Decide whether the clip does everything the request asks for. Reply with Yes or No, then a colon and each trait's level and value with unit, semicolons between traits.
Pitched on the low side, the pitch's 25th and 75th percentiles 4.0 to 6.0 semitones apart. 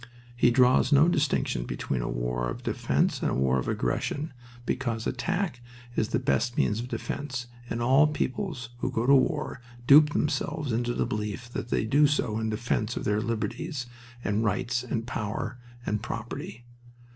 Yes: low, 120 Hz; average, 4.3 semitones